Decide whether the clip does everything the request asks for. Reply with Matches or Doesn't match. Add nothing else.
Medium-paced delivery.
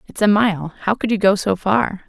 Doesn't match